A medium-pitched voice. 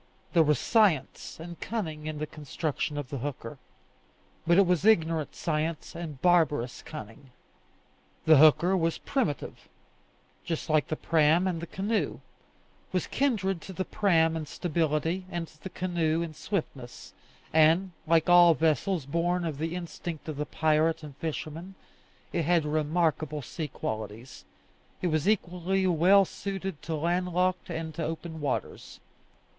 Yes: medium, 165 Hz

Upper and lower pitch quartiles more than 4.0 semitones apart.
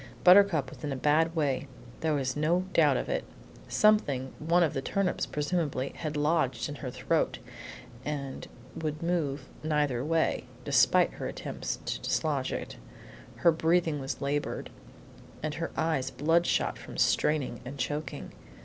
No: average, 3.2 semitones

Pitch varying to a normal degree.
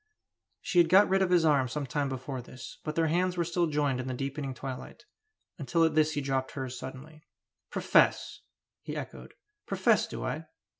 Yes: average, 3.8 semitones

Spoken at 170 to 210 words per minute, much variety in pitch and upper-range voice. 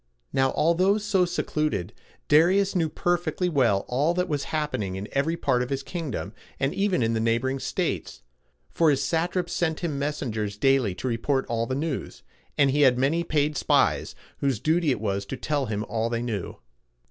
No: average, 180 wpm; wide, 5.7 semitones; medium, 140 Hz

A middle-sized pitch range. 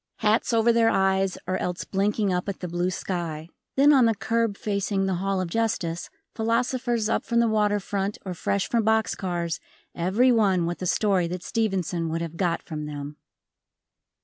Yes: average, 4.1 semitones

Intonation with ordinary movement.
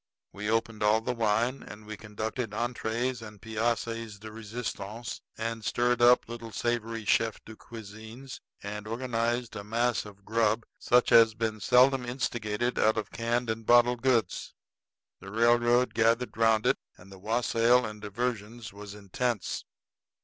No: narrow, 2.0 semitones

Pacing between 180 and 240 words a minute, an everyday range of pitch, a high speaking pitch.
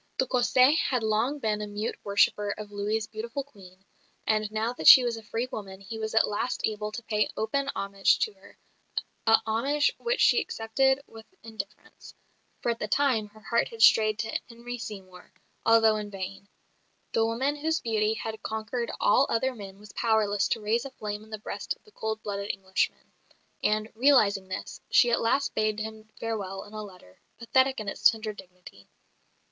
No: average, 185 wpm; narrow, 2.2 semitones; high, 220 Hz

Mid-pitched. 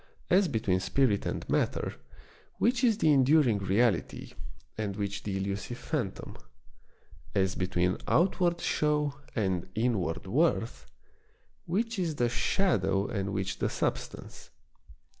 No: low, 115 Hz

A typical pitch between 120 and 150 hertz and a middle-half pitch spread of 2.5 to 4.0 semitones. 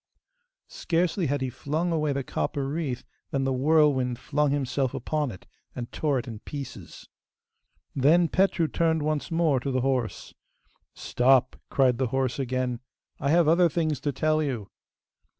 Yes: medium, 140 Hz; average, 3.3 semitones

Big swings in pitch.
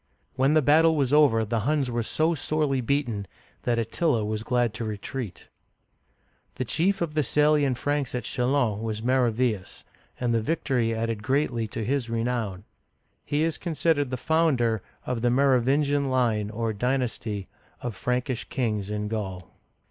No: average, 4.3 semitones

